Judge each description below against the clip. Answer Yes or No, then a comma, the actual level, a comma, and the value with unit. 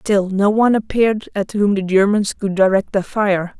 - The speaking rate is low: No, average, 200 wpm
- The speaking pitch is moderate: No, high, 200 Hz